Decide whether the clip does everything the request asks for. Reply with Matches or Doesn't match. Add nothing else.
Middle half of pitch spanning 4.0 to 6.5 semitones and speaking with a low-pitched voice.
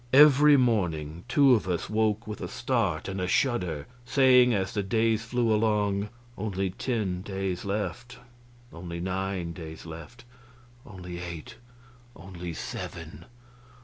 Matches